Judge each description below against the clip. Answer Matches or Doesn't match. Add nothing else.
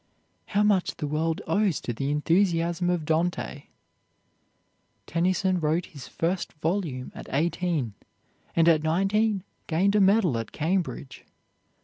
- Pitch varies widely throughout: Doesn't match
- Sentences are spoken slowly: Matches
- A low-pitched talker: Doesn't match